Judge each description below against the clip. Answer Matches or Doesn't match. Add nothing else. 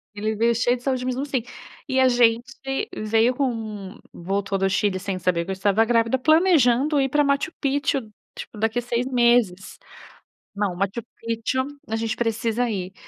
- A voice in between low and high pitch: Doesn't match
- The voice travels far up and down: Doesn't match